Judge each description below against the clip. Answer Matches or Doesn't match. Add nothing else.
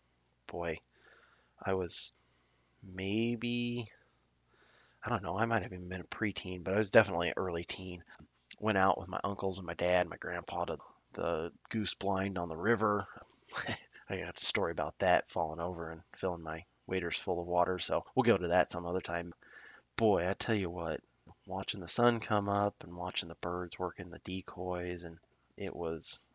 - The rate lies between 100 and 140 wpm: Doesn't match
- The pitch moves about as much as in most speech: Matches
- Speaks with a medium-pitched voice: Doesn't match